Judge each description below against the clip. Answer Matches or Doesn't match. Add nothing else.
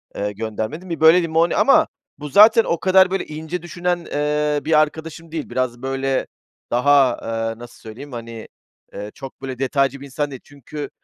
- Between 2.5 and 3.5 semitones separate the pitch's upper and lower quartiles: Doesn't match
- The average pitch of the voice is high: Doesn't match